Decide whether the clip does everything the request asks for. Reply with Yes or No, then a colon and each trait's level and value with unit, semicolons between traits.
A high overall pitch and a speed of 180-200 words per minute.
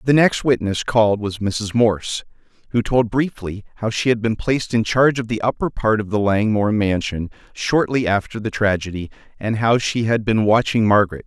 No: low, 110 Hz; average, 190 wpm